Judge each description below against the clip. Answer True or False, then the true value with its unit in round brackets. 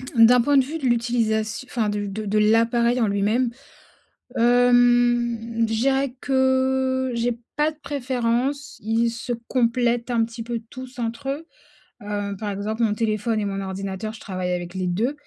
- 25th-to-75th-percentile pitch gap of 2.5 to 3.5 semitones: True (2.9 semitones)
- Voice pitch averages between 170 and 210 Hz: False (235 Hz)